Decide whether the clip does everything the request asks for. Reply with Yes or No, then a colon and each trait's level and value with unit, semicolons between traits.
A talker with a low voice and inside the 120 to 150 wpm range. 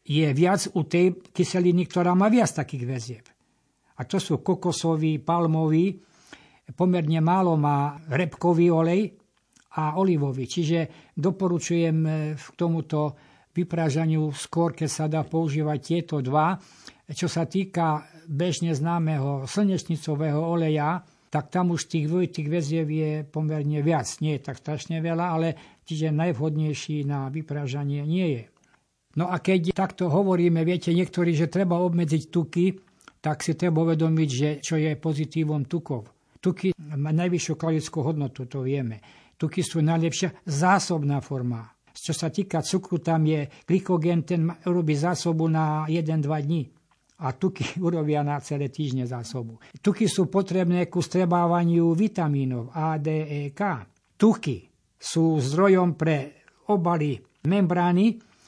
No: medium, 160 Hz; average, 130 wpm